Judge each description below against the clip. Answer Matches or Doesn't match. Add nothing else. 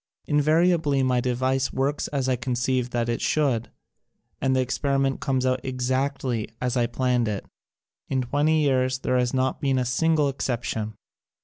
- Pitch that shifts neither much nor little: Doesn't match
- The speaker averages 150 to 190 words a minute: Matches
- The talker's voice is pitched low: Matches